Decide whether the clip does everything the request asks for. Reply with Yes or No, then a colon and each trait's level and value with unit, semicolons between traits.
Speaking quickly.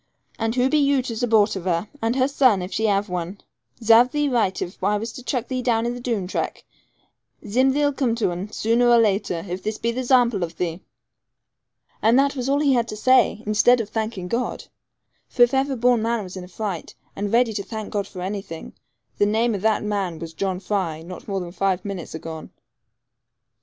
Yes: fast, 220 wpm